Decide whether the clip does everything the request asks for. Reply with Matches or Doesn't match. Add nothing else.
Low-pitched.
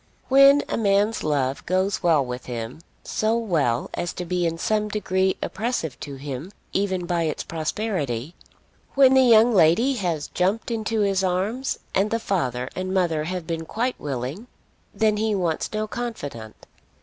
Doesn't match